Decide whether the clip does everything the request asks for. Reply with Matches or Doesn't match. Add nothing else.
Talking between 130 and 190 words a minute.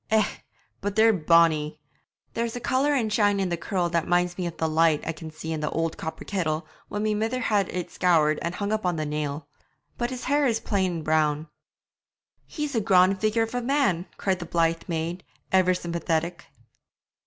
Doesn't match